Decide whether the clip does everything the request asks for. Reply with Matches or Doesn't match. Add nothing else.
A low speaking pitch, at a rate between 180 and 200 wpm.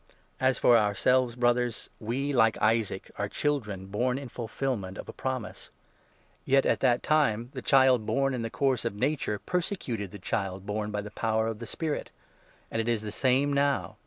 Matches